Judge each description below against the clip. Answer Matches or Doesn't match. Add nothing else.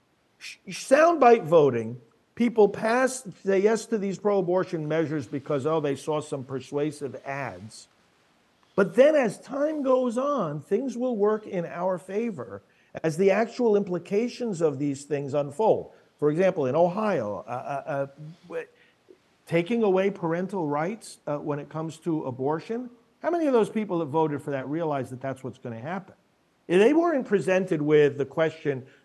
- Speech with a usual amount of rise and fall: Doesn't match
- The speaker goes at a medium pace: Matches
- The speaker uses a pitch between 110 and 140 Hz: Doesn't match